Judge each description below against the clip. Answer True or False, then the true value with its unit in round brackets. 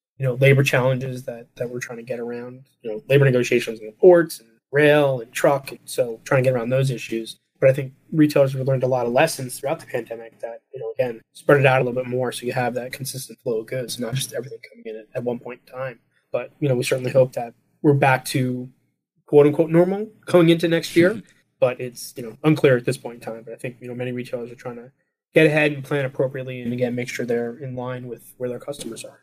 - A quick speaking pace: True (260 wpm)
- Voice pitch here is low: True (130 Hz)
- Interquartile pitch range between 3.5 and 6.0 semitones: False (2.9 semitones)